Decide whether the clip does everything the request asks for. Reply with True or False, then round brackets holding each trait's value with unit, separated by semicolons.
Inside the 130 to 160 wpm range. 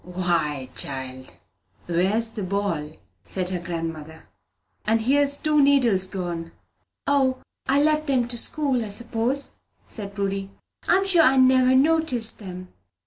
True (135 wpm)